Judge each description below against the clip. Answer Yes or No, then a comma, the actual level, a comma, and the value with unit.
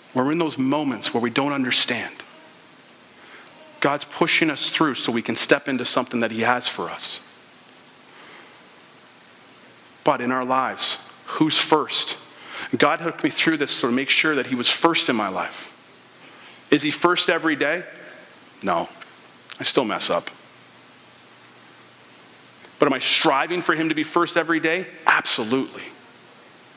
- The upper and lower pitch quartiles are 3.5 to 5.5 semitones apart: Yes, average, 5.1 semitones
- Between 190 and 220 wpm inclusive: No, average, 150 wpm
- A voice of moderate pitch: Yes, medium, 150 Hz